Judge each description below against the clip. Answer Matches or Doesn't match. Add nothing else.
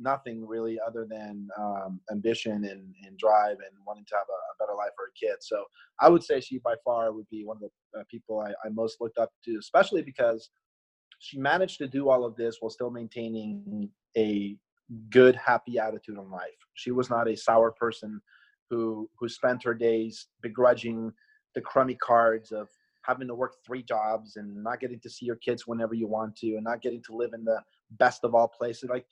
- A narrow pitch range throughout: Matches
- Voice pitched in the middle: Doesn't match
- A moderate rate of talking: Doesn't match